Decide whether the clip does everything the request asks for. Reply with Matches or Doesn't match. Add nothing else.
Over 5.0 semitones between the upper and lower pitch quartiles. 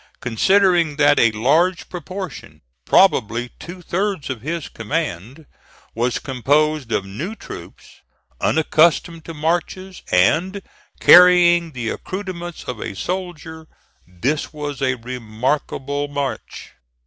Matches